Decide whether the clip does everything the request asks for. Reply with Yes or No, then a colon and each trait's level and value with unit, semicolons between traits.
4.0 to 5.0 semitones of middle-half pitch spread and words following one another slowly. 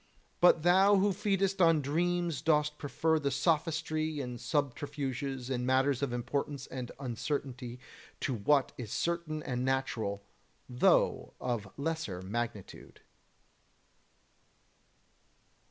Yes: average, 4.5 semitones; slow, 105 wpm